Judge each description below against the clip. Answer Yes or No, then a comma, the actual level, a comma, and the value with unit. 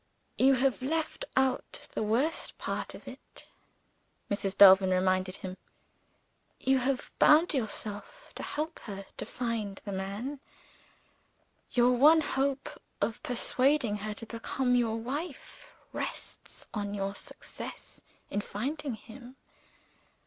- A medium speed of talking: No, slow, 120 wpm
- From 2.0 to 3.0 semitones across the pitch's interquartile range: No, average, 5.0 semitones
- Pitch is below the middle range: No, high, 240 Hz